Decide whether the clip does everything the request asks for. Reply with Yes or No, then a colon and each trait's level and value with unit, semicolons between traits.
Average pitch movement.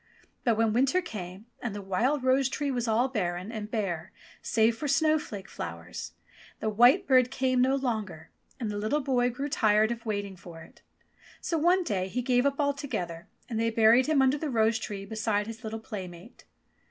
Yes: average, 4.4 semitones